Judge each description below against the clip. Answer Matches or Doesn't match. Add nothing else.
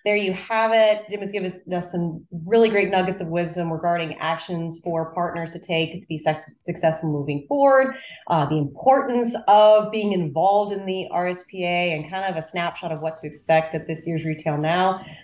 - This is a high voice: Doesn't match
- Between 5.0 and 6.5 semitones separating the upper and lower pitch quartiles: Doesn't match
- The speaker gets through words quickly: Doesn't match